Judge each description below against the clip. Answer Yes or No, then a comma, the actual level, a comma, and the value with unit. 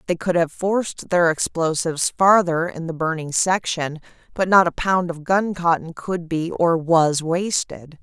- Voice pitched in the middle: Yes, medium, 170 Hz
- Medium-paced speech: Yes, average, 165 wpm